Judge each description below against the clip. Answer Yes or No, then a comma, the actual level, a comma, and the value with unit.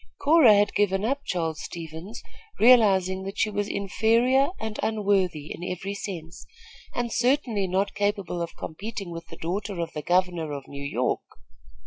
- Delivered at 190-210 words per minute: No, average, 155 wpm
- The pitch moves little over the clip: No, average, 4.3 semitones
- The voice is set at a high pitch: Yes, high, 195 Hz